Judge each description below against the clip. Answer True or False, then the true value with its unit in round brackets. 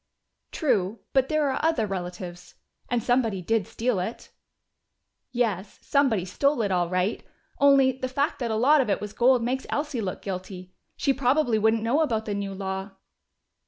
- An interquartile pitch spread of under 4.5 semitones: False (5.4 semitones)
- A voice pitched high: True (225 Hz)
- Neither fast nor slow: True (170 wpm)